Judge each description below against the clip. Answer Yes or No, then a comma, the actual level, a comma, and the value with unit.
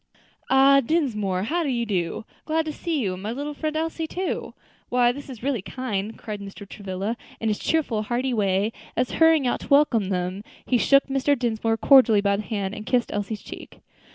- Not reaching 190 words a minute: No, average, 200 wpm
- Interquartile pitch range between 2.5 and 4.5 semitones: No, average, 5.2 semitones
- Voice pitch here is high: Yes, high, 235 Hz